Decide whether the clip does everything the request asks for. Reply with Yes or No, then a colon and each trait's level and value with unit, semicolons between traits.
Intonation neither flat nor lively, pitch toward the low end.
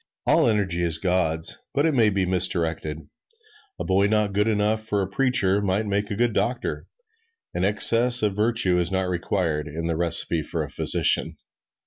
Yes: average, 3.7 semitones; low, 100 Hz